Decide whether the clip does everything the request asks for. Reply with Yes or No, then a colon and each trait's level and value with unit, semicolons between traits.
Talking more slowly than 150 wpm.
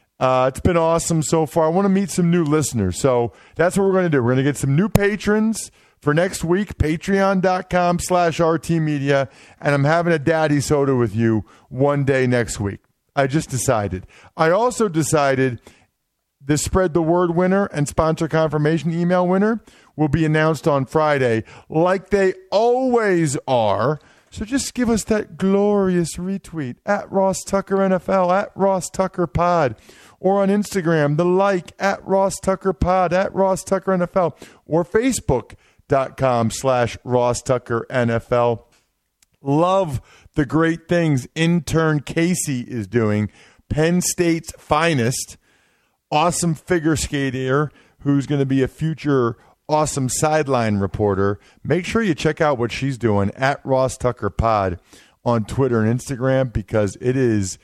No: average, 155 wpm